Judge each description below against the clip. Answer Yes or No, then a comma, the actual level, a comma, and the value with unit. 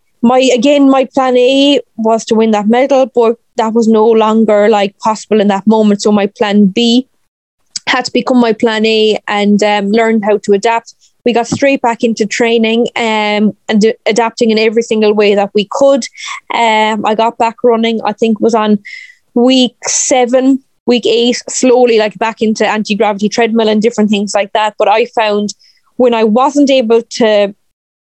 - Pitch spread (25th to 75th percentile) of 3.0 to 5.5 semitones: No, narrow, 2.4 semitones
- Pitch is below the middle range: No, high, 225 Hz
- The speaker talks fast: No, average, 185 wpm